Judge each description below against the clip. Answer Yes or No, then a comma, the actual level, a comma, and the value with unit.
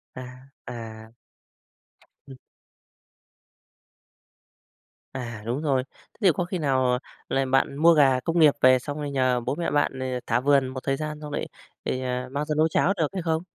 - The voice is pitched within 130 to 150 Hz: Yes, low, 135 Hz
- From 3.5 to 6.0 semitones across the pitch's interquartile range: No, average, 3.1 semitones